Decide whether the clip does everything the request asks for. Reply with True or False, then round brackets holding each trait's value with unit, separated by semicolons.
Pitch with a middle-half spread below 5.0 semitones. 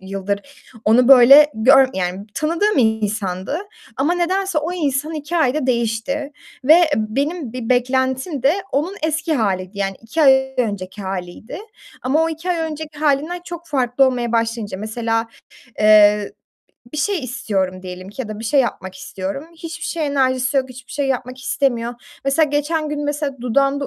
False (5.4 semitones)